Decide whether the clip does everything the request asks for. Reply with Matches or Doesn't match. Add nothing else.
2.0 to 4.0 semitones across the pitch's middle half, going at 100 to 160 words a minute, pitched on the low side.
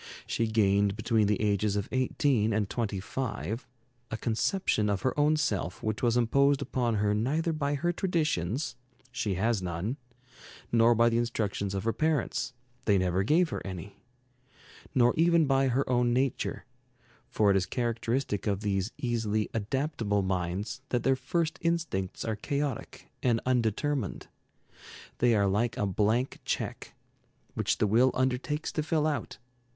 Doesn't match